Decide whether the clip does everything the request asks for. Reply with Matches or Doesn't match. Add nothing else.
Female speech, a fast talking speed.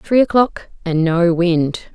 Doesn't match